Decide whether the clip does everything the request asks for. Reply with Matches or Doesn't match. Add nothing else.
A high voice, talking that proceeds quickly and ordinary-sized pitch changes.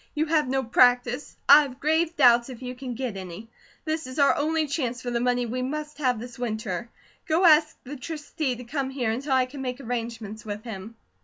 Matches